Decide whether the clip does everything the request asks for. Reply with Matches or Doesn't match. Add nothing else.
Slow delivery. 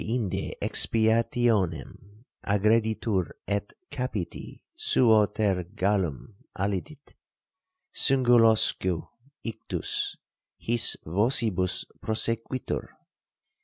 Matches